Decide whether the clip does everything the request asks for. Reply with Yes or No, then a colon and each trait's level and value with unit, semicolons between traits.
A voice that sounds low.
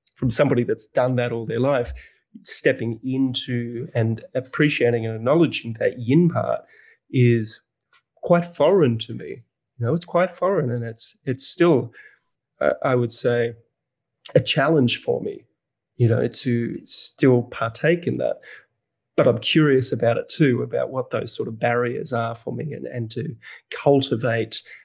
Yes: low, 120 Hz